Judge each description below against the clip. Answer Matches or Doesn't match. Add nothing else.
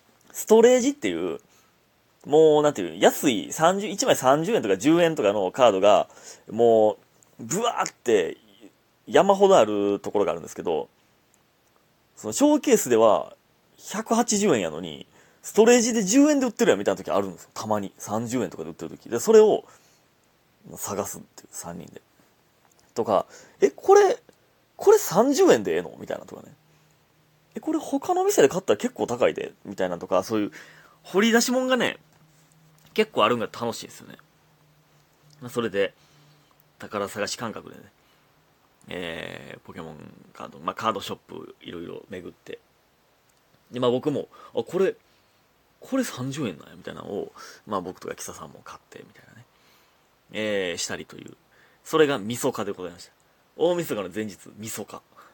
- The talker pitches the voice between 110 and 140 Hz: Doesn't match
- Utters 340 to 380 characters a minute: Doesn't match